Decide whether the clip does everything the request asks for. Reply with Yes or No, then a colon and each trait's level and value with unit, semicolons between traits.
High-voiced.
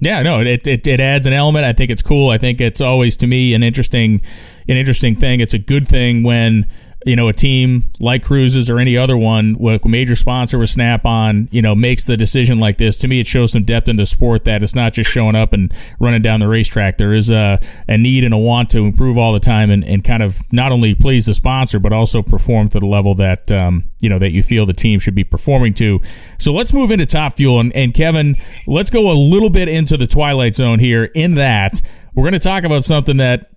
No: low, 120 Hz